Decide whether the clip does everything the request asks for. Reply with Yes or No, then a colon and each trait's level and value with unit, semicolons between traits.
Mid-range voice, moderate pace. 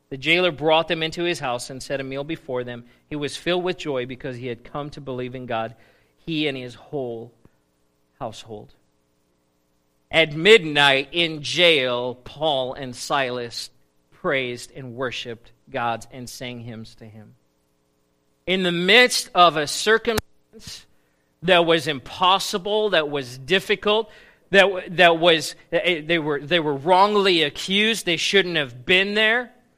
Yes: medium, 145 Hz; average, 145 wpm